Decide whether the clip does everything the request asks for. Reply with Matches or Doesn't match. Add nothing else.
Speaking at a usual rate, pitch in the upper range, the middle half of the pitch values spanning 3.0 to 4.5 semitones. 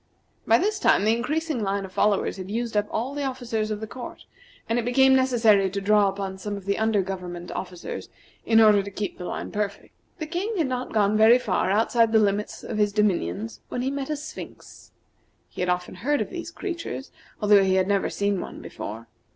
Doesn't match